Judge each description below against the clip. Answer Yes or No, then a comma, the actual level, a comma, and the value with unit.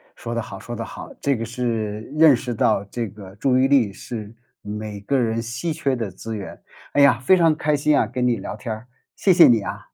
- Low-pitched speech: Yes, low, 115 Hz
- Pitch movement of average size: Yes, average, 4.1 semitones